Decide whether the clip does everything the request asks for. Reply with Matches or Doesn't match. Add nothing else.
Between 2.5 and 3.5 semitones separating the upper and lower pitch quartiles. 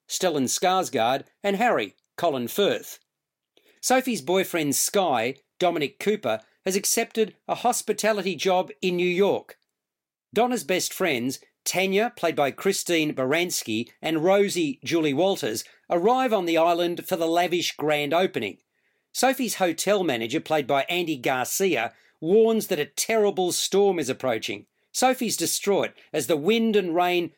Doesn't match